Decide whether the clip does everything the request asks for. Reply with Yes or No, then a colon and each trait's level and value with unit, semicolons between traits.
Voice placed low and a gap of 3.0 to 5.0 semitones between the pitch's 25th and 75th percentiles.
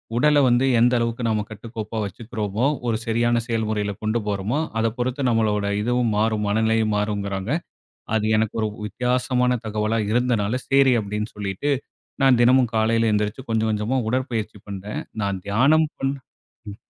No: low, 110 Hz; narrow, 2.6 semitones